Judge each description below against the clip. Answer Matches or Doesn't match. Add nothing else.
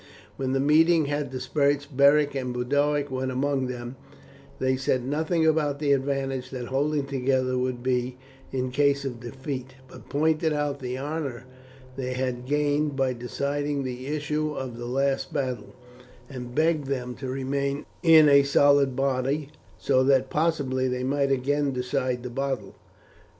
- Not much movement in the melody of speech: Matches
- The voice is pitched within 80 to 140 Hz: Matches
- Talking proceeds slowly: Doesn't match